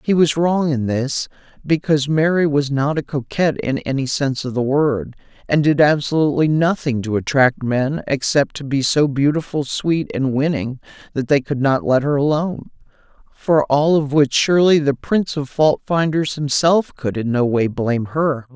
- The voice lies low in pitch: No, medium, 145 Hz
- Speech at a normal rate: Yes, average, 180 wpm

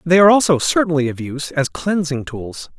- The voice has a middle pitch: Yes, medium, 155 Hz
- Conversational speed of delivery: Yes, average, 195 wpm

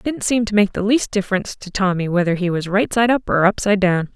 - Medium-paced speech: No, fast, 275 wpm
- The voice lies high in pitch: Yes, high, 200 Hz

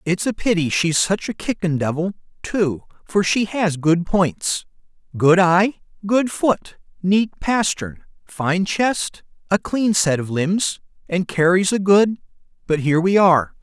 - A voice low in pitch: No, medium, 185 Hz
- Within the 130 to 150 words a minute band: Yes, average, 145 wpm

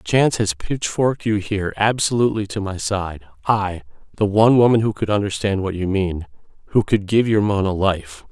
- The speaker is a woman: No, male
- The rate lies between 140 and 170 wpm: No, average, 180 wpm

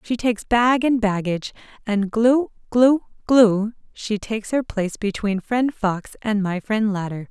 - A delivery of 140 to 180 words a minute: Yes, average, 165 wpm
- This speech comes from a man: No, female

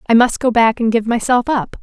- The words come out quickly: Yes, fast, 260 wpm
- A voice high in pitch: Yes, high, 235 Hz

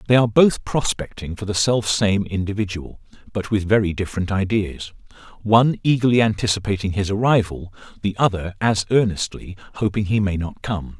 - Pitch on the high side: No, low, 100 Hz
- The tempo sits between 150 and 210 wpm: No, average, 140 wpm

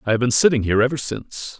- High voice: No, low, 125 Hz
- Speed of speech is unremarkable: No, fast, 265 wpm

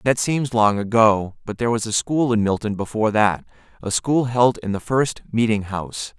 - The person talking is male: Yes, male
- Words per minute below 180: No, fast, 205 wpm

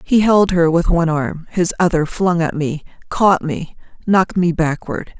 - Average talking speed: Yes, average, 185 wpm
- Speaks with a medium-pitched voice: Yes, medium, 170 Hz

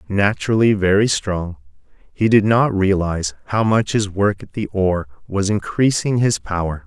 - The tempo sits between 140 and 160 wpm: Yes, average, 155 wpm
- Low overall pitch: Yes, low, 100 Hz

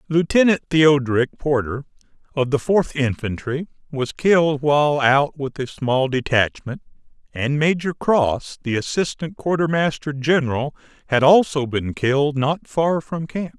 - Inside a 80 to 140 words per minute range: Yes, slow, 135 wpm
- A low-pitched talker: No, medium, 145 Hz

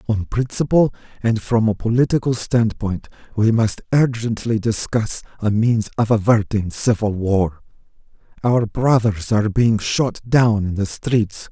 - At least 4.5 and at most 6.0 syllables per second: No, 4.2 syllables/s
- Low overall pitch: Yes, low, 110 Hz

